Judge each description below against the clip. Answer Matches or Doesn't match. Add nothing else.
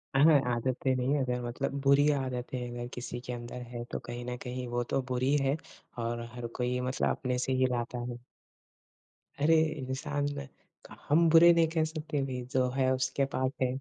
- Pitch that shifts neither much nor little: Doesn't match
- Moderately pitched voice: Doesn't match